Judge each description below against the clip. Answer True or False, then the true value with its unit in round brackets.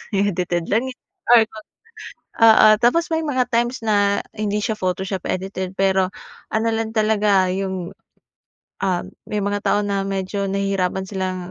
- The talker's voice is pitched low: False (200 Hz)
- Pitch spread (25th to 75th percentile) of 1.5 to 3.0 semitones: True (2.5 semitones)